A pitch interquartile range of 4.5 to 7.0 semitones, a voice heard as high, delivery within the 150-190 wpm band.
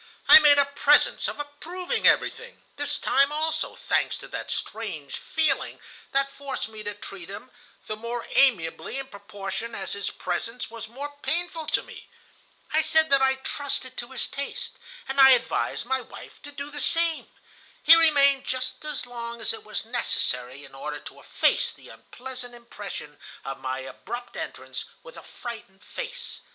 Yes: average, 5.2 semitones; very high, 260 Hz; average, 170 wpm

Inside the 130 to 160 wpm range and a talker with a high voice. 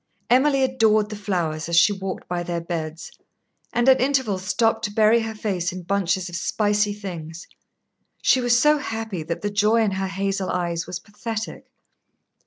No: average, 175 wpm; high, 205 Hz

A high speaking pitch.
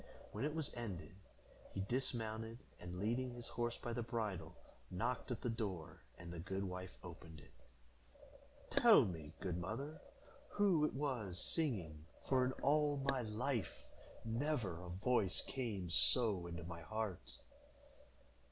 No: low, 110 Hz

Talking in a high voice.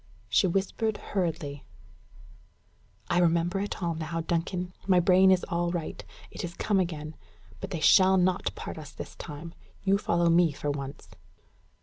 No: medium, 175 Hz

